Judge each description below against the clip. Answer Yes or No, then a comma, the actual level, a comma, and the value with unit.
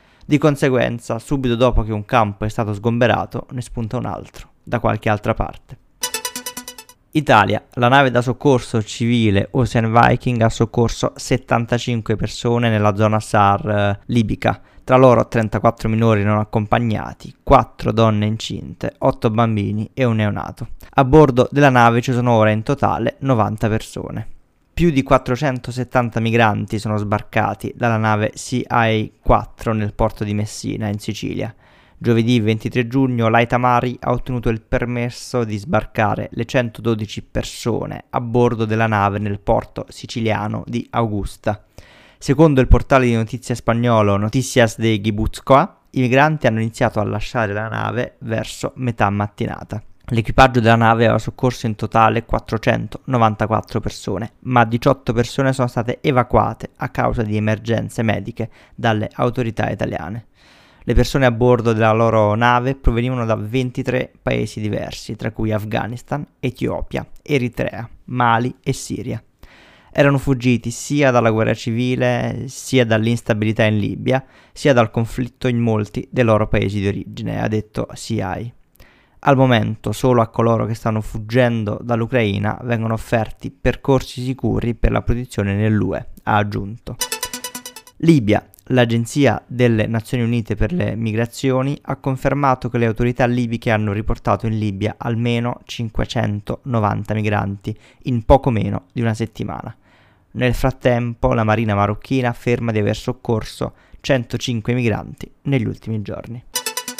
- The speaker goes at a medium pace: Yes, average, 135 wpm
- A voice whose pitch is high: No, low, 115 Hz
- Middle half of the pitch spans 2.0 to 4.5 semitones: Yes, narrow, 2.6 semitones